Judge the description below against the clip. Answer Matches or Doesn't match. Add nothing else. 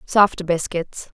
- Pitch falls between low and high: Matches